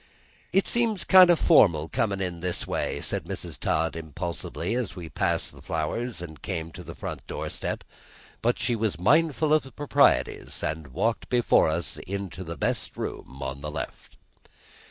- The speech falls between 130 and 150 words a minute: No, average, 170 wpm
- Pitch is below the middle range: Yes, very low, 95 Hz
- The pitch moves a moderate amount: No, wide, 7.5 semitones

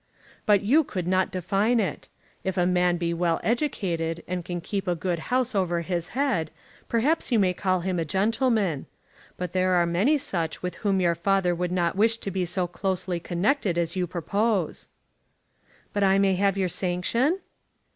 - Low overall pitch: No, medium, 185 Hz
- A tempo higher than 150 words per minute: Yes, average, 180 wpm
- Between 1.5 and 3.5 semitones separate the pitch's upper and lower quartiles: Yes, average, 2.8 semitones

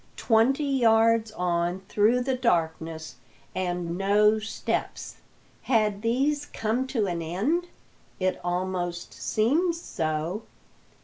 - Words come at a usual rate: No, slow, 105 wpm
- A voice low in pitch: No, high, 210 Hz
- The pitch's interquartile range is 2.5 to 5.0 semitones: No, wide, 5.6 semitones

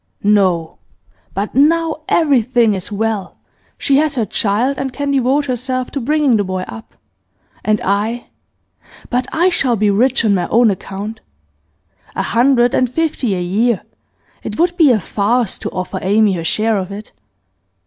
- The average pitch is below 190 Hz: No, high, 230 Hz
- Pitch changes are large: No, average, 4.9 semitones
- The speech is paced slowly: No, average, 160 wpm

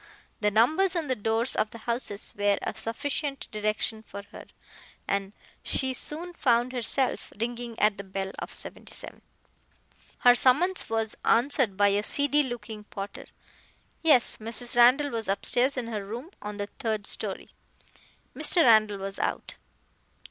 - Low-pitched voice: No, high, 230 Hz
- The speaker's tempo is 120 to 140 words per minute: No, average, 150 wpm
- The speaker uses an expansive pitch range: No, average, 3.9 semitones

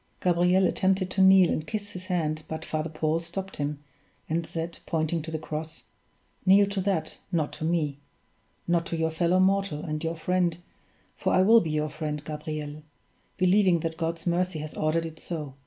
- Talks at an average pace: Yes, average, 185 wpm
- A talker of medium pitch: Yes, medium, 165 Hz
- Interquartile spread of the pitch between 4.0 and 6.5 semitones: No, average, 3.0 semitones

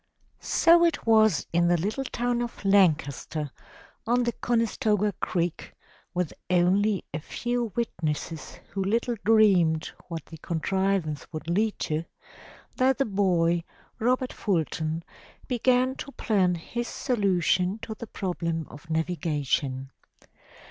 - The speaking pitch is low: No, high, 190 Hz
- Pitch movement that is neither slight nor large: No, wide, 5.7 semitones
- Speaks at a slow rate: Yes, slow, 120 wpm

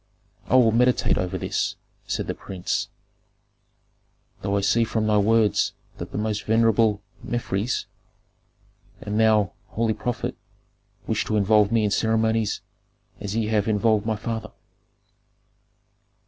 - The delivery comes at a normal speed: No, slow, 130 wpm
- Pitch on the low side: Yes, low, 110 Hz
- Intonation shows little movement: Yes, narrow, 1.5 semitones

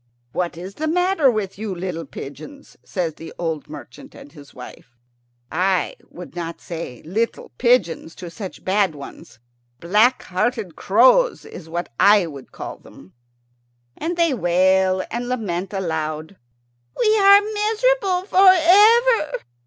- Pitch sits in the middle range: No, high, 195 Hz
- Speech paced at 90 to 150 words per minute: Yes, slow, 135 wpm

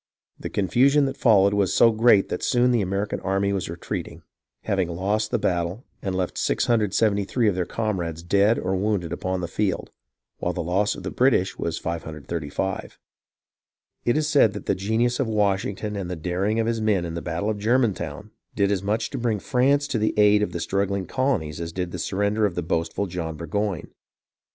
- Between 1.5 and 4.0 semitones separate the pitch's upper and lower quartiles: Yes, average, 3.6 semitones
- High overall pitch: No, low, 100 Hz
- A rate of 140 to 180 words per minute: No, average, 195 wpm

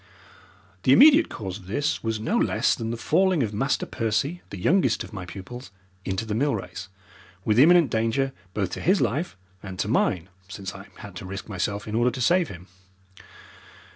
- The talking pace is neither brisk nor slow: Yes, average, 190 wpm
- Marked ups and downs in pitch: Yes, wide, 6.4 semitones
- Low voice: Yes, low, 110 Hz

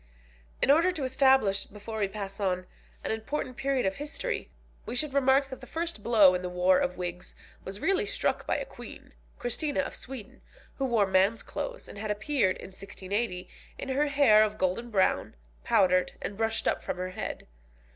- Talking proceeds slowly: No, average, 185 wpm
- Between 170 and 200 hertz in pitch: No, high, 220 Hz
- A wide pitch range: Yes, wide, 6.0 semitones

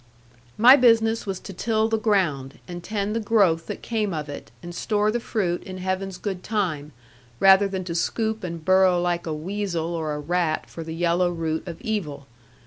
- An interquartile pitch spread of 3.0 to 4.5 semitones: Yes, average, 4.0 semitones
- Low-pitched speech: No, medium, 185 Hz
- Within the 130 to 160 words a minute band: No, average, 195 wpm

